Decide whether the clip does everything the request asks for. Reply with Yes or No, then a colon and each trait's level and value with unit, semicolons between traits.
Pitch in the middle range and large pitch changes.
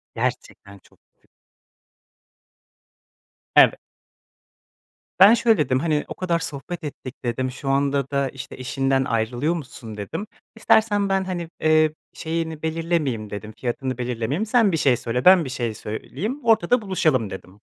Yes: medium, 145 Hz; wide, 5.7 semitones